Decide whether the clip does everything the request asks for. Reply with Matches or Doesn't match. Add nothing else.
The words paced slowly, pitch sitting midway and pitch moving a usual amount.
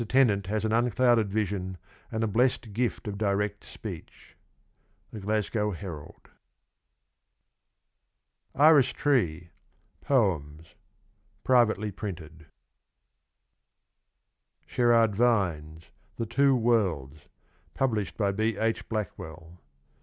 Doesn't match